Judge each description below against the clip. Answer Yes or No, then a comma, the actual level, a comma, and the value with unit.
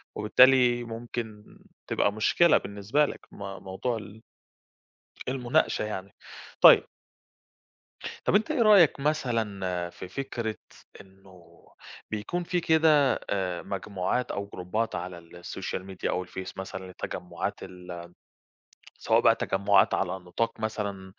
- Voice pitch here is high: No, low, 105 Hz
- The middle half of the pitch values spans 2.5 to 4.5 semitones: No, average, 4.9 semitones